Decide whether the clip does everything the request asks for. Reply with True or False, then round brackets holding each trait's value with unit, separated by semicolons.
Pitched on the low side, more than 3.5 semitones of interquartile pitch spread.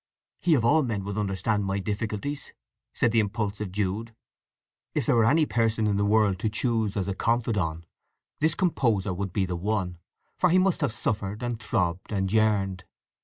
False (105 Hz; 2.9 semitones)